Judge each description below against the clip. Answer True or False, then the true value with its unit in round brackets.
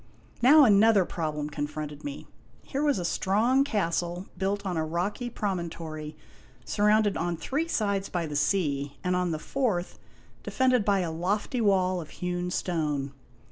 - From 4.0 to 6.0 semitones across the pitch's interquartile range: True (4.5 semitones)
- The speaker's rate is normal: True (155 wpm)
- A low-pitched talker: False (180 Hz)